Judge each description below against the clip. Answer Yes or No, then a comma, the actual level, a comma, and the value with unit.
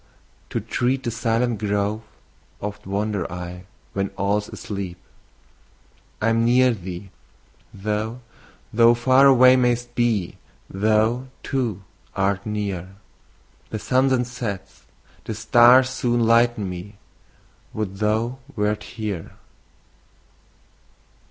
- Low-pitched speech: Yes, low, 110 Hz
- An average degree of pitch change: Yes, average, 3.2 semitones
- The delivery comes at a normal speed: No, slow, 105 wpm